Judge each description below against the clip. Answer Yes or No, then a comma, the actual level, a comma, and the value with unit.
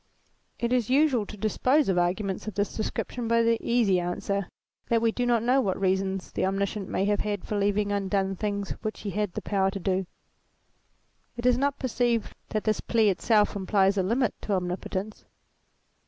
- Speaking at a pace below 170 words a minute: No, average, 190 wpm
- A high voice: Yes, high, 205 Hz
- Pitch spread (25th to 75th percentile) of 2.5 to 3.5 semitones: Yes, average, 3.1 semitones